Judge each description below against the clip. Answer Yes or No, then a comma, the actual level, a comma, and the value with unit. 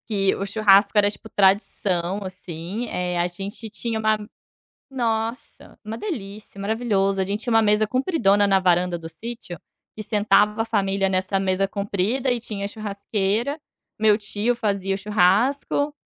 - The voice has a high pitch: Yes, high, 205 Hz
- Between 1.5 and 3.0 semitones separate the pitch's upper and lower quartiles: Yes, narrow, 2.4 semitones